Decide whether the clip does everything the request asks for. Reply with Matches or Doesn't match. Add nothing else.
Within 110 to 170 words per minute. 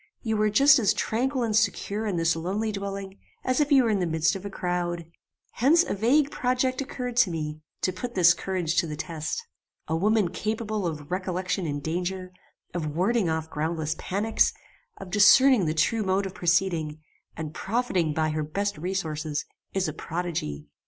Doesn't match